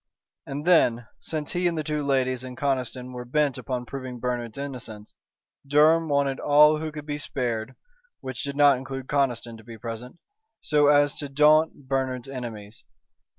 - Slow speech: No, average, 165 wpm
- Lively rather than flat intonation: No, average, 2.9 semitones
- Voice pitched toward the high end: No, low, 135 Hz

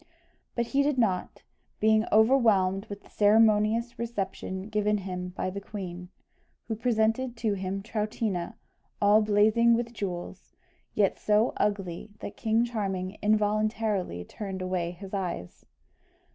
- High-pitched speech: Yes, high, 210 Hz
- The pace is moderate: No, slow, 130 wpm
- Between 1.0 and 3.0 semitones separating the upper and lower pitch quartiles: Yes, average, 2.7 semitones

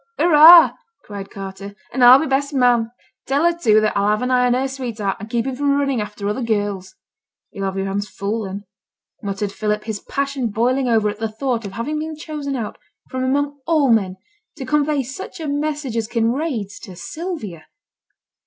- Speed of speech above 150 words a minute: Yes, average, 195 wpm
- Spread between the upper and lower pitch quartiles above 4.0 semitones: Yes, average, 5.2 semitones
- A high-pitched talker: Yes, high, 240 Hz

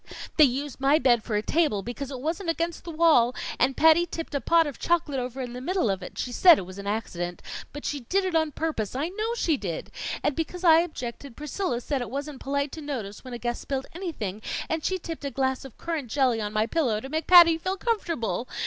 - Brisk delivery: Yes, fast, 240 wpm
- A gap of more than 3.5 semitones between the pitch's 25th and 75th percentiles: Yes, wide, 5.4 semitones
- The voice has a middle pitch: No, very high, 280 Hz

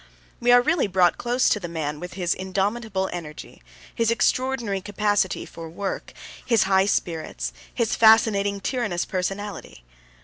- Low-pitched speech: No, high, 200 Hz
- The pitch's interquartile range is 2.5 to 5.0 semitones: Yes, average, 4.1 semitones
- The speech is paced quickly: No, average, 140 wpm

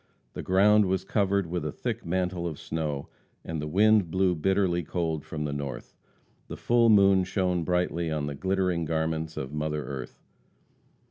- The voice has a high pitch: No, very low, 85 Hz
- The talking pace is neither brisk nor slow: Yes, average, 165 wpm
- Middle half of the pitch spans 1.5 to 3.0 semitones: No, average, 3.5 semitones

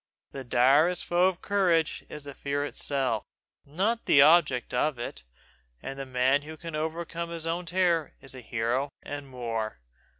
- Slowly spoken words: No, average, 165 wpm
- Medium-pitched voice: Yes, medium, 145 Hz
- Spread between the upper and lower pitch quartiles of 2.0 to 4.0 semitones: No, average, 4.5 semitones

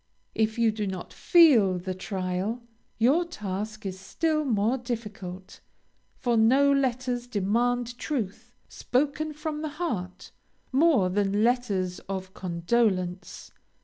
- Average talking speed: No, slow, 115 wpm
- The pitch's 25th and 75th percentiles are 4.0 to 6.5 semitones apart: Yes, average, 5.2 semitones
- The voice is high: Yes, high, 225 Hz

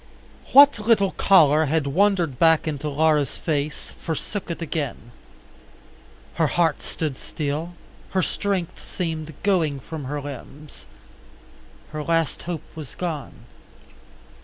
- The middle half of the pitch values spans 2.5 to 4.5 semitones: Yes, average, 3.0 semitones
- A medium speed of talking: No, slow, 115 wpm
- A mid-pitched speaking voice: Yes, medium, 160 Hz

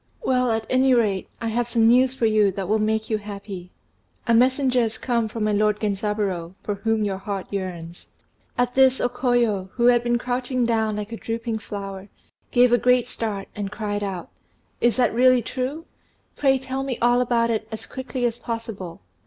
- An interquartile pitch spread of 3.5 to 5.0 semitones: No, average, 3.0 semitones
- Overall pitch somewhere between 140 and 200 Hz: No, high, 225 Hz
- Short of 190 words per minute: No, average, 195 wpm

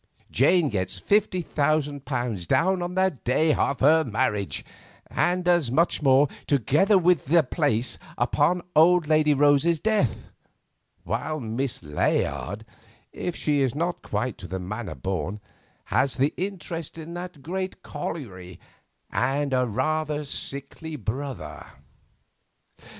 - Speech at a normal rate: No, slow, 125 wpm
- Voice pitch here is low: No, medium, 145 Hz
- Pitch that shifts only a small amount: No, average, 5.3 semitones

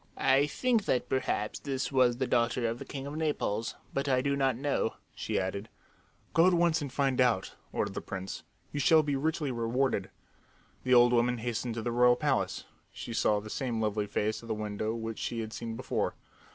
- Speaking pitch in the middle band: No, low, 125 Hz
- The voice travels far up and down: No, average, 3.6 semitones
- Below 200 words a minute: No, fast, 205 wpm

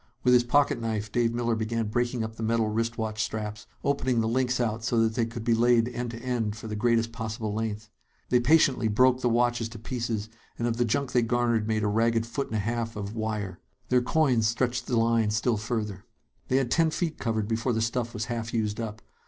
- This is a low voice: Yes, low, 115 Hz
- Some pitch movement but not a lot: No, narrow, 1.7 semitones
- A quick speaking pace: Yes, fast, 225 wpm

